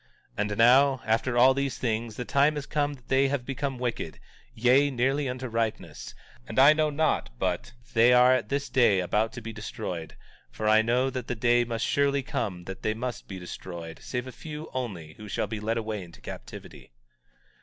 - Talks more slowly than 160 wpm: No, average, 200 wpm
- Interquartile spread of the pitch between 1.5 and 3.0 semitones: No, average, 3.8 semitones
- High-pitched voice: No, low, 120 Hz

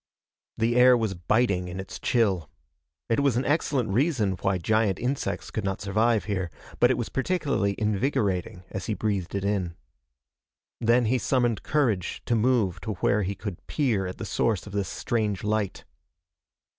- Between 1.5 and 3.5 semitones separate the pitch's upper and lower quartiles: No, average, 3.9 semitones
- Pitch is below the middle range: Yes, low, 110 Hz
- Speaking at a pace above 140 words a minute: Yes, average, 170 wpm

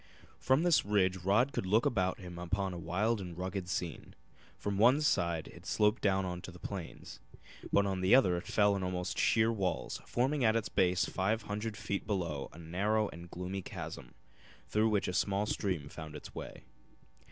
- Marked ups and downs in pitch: No, average, 3.1 semitones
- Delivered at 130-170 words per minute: No, average, 185 wpm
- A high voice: No, very low, 95 Hz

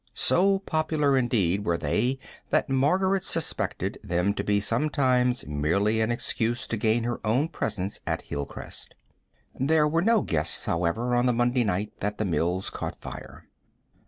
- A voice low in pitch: Yes, low, 120 Hz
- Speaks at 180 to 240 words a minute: No, average, 155 wpm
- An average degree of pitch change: No, wide, 5.8 semitones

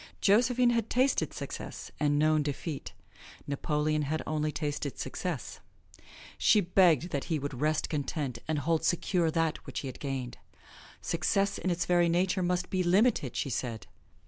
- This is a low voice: No, medium, 155 Hz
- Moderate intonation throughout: Yes, average, 3.8 semitones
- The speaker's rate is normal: Yes, average, 155 wpm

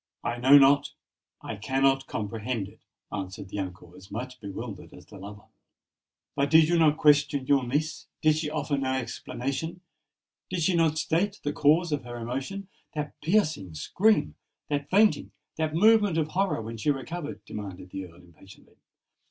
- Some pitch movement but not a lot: No, wide, 6.1 semitones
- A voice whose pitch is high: No, medium, 140 Hz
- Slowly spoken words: No, average, 150 wpm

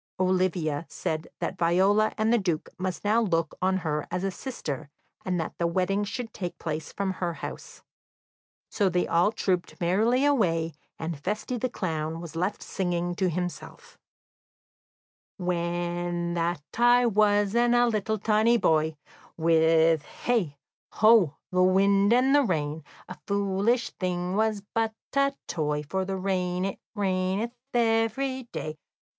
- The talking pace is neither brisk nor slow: Yes, average, 145 wpm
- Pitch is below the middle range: No, medium, 185 Hz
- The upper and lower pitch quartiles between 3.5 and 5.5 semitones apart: Yes, average, 4.2 semitones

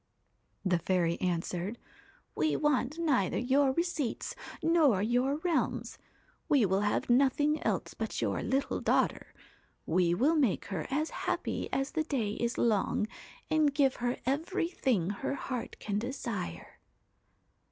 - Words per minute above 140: No, slow, 135 wpm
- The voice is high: Yes, very high, 255 Hz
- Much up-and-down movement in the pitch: Yes, wide, 6.3 semitones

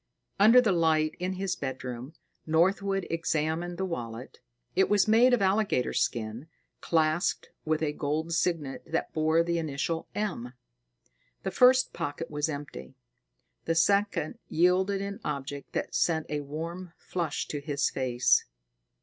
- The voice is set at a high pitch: No, medium, 165 Hz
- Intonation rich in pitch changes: No, average, 4.4 semitones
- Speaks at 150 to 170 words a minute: No, average, 140 wpm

